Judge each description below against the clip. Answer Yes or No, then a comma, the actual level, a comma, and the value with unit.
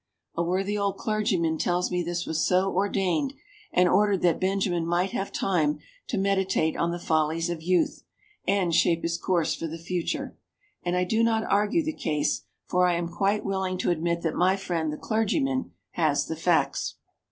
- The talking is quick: No, average, 185 wpm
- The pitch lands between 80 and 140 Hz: No, medium, 180 Hz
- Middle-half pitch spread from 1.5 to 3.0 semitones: Yes, average, 2.7 semitones